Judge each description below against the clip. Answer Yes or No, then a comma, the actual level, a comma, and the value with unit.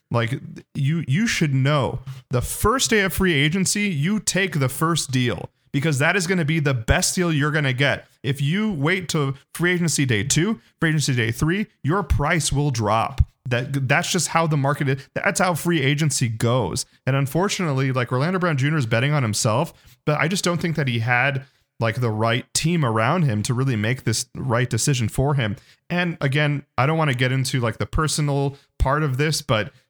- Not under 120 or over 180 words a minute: No, fast, 205 wpm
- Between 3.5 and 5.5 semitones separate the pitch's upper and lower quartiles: Yes, average, 4.4 semitones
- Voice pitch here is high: No, medium, 140 Hz